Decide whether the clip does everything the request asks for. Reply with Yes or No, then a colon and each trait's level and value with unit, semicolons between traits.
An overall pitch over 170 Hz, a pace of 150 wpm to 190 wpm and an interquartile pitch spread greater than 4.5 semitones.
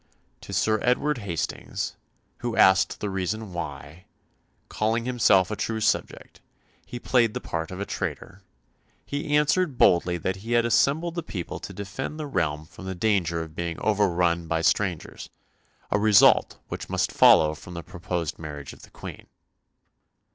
No: very low, 95 Hz; average, 160 wpm; wide, 5.5 semitones